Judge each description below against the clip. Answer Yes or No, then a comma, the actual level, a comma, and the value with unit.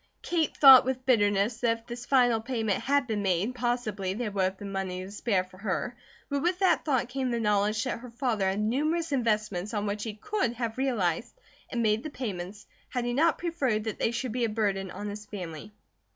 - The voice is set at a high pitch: Yes, high, 225 Hz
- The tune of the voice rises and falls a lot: No, average, 3.9 semitones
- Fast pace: Yes, fast, 215 wpm